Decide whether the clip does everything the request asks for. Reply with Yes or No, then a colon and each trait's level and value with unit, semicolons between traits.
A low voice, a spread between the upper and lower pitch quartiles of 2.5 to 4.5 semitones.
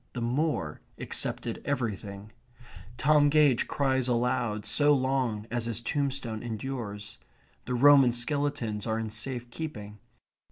Yes: low, 120 Hz; average, 4.1 semitones